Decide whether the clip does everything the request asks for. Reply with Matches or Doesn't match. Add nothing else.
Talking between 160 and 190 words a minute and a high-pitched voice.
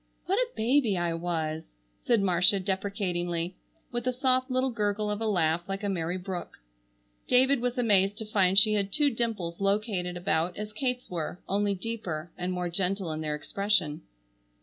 Matches